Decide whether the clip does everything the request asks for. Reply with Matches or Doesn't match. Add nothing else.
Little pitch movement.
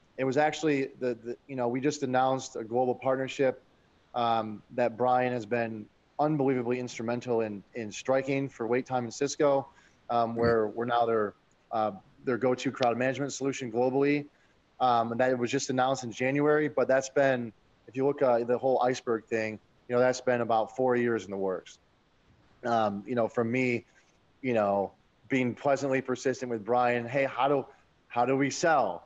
Matches